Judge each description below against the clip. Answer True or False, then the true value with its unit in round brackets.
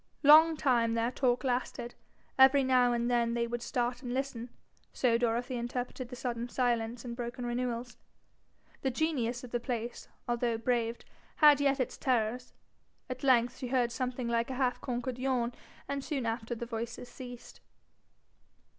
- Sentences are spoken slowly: False (155 wpm)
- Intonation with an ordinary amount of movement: False (1.5 semitones)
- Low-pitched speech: False (245 Hz)